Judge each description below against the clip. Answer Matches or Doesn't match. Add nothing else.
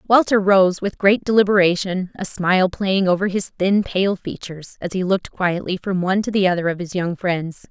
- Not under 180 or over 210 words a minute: Matches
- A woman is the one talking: Matches